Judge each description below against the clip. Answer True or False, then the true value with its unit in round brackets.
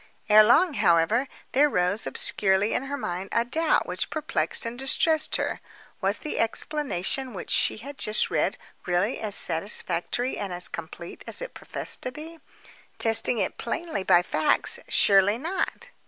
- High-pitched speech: True (225 Hz)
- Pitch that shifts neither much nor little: False (7.2 semitones)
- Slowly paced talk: False (155 wpm)